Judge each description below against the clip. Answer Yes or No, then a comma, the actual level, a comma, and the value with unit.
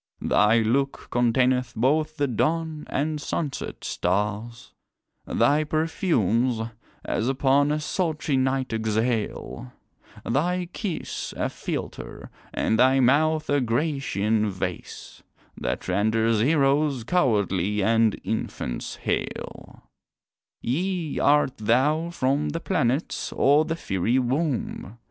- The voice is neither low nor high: No, low, 130 Hz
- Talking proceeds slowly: Yes, slow, 105 wpm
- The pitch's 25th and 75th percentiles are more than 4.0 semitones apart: Yes, average, 5.2 semitones